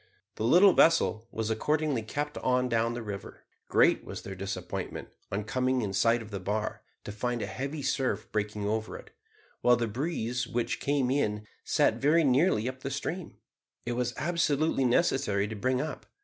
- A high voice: No, low, 125 Hz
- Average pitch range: Yes, average, 4.4 semitones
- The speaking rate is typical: Yes, average, 175 wpm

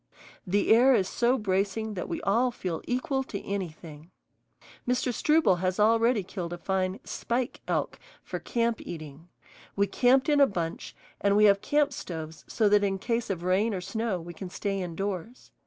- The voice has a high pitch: Yes, high, 200 Hz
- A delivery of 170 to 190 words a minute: Yes, average, 175 wpm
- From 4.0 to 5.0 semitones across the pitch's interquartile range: Yes, average, 4.4 semitones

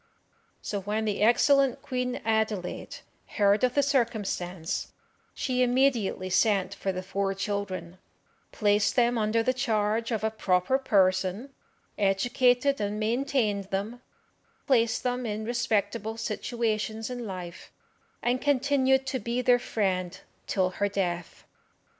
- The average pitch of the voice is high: Yes, high, 220 Hz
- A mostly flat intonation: No, average, 3.9 semitones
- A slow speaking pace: Yes, slow, 125 wpm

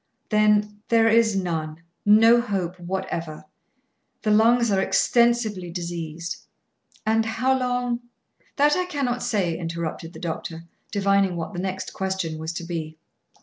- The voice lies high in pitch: Yes, high, 195 Hz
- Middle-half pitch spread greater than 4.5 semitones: Yes, average, 5.0 semitones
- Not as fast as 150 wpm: Yes, average, 140 wpm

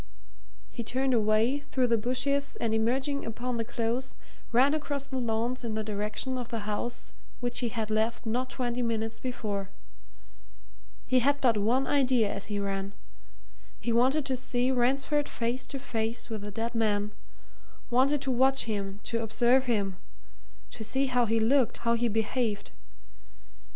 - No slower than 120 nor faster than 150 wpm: No, average, 160 wpm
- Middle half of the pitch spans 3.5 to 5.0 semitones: No, average, 2.8 semitones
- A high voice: Yes, high, 235 Hz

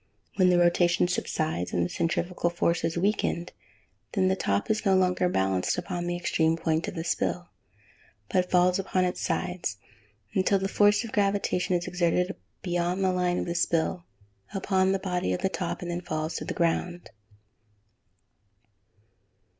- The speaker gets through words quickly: No, average, 170 wpm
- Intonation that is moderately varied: No, narrow, 1.6 semitones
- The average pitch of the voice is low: No, medium, 180 Hz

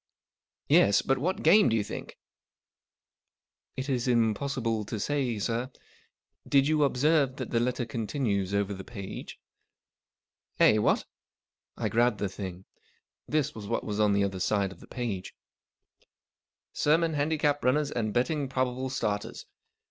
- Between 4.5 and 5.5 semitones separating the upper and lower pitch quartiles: Yes, average, 5.1 semitones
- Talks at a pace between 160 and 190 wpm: Yes, average, 165 wpm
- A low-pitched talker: Yes, low, 120 Hz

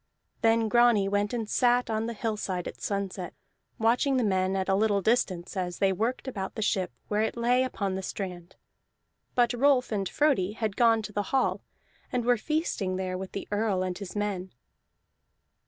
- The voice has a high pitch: Yes, high, 210 Hz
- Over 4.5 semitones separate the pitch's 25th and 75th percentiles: No, average, 3.8 semitones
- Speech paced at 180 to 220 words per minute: Yes, average, 185 wpm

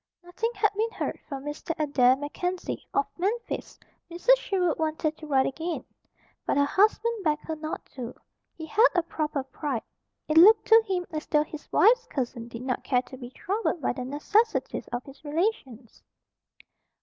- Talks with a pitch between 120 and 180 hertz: No, very high, 310 Hz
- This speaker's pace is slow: No, average, 175 wpm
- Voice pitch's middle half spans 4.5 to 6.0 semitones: Yes, wide, 5.4 semitones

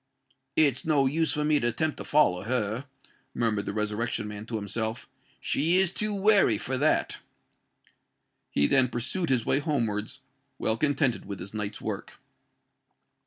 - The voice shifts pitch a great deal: Yes, wide, 5.9 semitones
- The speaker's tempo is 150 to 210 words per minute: Yes, average, 155 wpm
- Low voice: Yes, low, 125 Hz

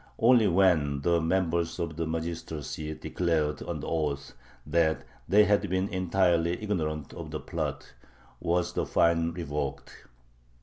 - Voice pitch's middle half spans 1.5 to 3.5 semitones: Yes, average, 2.8 semitones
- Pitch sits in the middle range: No, very low, 85 Hz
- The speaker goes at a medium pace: No, slow, 130 wpm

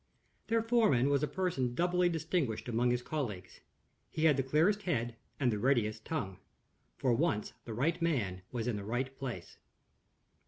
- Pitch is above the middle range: No, low, 130 Hz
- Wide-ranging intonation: Yes, wide, 6.1 semitones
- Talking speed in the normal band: Yes, average, 165 wpm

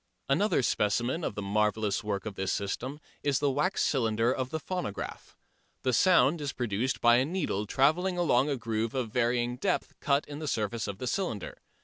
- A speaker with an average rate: Yes, average, 190 wpm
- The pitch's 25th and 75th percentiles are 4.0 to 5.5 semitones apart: Yes, average, 5.1 semitones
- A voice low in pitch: Yes, low, 125 Hz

